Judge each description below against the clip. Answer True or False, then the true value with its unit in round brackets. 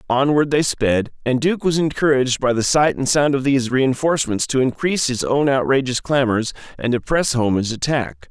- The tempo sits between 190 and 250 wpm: True (195 wpm)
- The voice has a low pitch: True (130 Hz)